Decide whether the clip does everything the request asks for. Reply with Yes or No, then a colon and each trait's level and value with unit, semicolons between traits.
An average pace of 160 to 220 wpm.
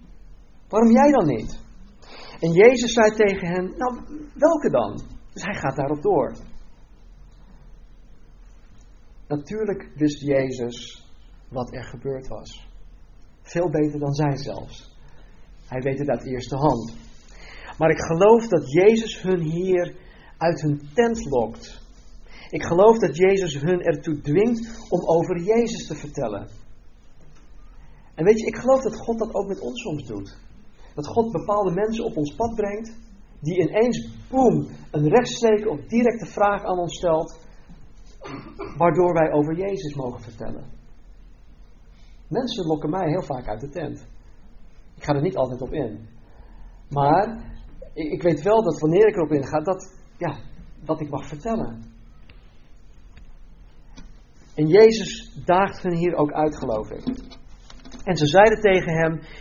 No: average, 140 wpm